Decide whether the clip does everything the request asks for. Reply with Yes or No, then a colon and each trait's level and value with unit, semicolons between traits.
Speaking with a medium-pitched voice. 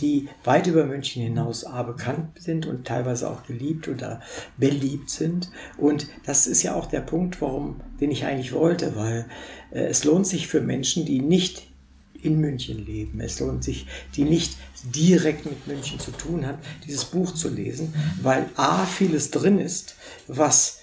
Yes: medium, 145 Hz